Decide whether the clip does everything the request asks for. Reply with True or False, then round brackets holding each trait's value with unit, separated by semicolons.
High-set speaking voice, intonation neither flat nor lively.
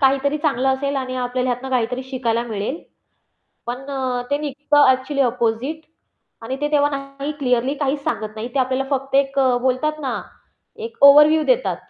False (270 Hz; 2.2 semitones)